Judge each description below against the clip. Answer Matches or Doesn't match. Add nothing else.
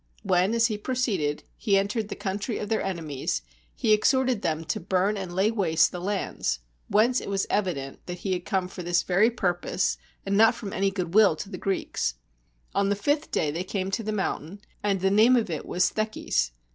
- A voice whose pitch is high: Matches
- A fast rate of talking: Matches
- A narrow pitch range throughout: Doesn't match